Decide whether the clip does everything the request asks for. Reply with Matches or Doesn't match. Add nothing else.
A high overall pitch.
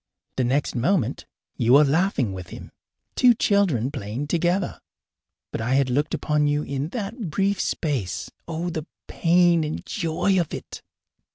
Doesn't match